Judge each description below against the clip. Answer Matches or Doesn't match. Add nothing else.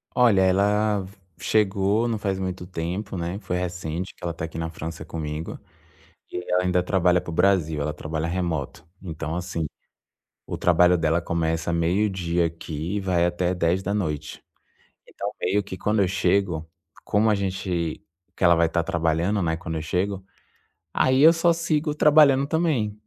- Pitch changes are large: Doesn't match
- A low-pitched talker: Matches